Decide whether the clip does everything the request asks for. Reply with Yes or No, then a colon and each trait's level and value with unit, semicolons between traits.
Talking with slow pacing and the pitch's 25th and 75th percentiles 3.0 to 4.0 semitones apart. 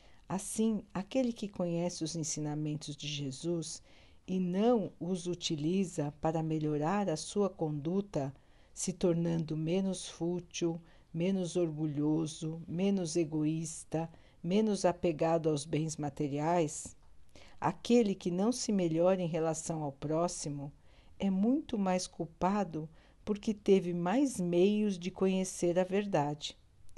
Yes: slow, 115 wpm; average, 3.4 semitones